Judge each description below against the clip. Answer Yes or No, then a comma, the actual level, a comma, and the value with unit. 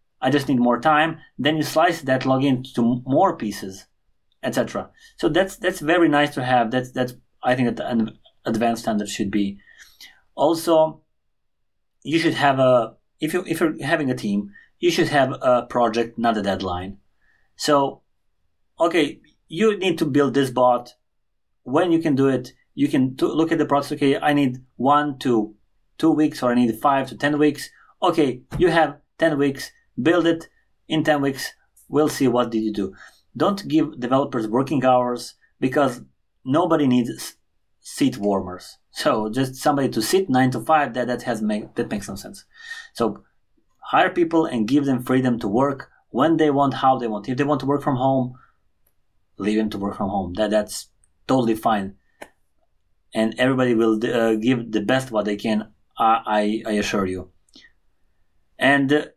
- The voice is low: Yes, low, 130 Hz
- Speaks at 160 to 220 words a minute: Yes, average, 180 wpm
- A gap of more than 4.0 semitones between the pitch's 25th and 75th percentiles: Yes, wide, 5.4 semitones